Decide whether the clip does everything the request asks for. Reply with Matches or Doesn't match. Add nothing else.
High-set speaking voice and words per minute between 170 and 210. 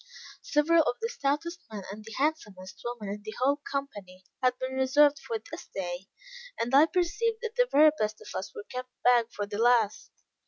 Matches